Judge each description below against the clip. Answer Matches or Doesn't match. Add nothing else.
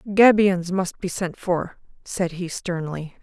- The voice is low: Doesn't match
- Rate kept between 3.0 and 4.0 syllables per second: Matches